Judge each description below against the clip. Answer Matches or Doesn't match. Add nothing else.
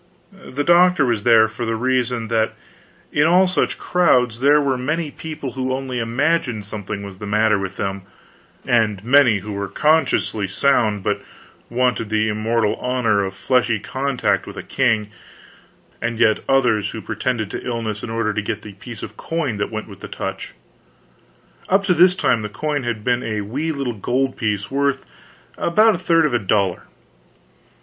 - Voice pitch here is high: Doesn't match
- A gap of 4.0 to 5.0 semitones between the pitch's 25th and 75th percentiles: Matches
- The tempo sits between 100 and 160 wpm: Doesn't match